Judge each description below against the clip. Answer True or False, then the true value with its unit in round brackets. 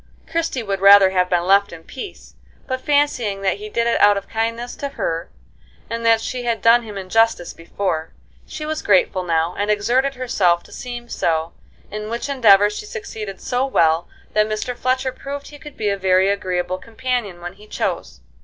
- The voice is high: True (210 Hz)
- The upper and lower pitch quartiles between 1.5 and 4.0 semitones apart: False (4.7 semitones)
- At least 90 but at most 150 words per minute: False (190 wpm)